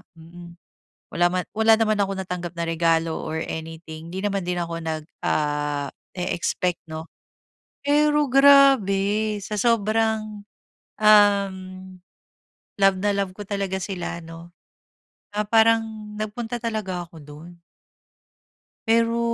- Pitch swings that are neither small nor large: Yes, average, 4.3 semitones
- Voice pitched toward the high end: Yes, high, 195 Hz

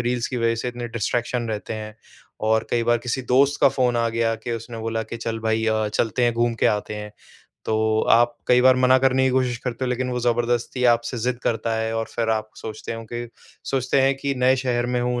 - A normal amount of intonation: No, narrow, 1.8 semitones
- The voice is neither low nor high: No, low, 120 Hz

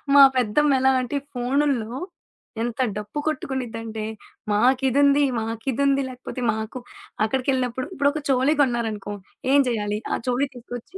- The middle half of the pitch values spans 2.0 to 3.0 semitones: No, average, 3.5 semitones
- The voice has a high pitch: Yes, very high, 255 Hz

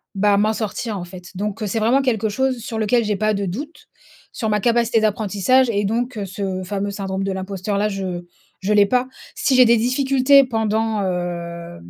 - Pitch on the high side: Yes, high, 210 Hz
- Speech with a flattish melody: No, average, 3.2 semitones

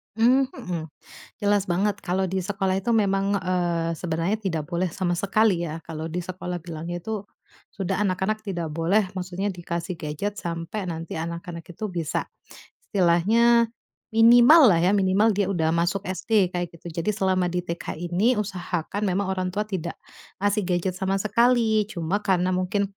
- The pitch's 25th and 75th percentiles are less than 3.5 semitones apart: Yes, average, 3.0 semitones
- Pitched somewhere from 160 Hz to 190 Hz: Yes, medium, 185 Hz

